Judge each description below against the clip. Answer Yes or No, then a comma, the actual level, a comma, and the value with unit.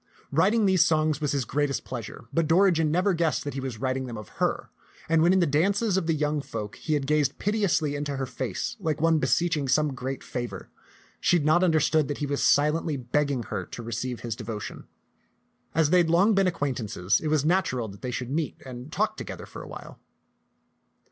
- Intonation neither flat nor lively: Yes, average, 4.2 semitones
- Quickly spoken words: Yes, fast, 210 wpm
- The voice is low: No, medium, 150 Hz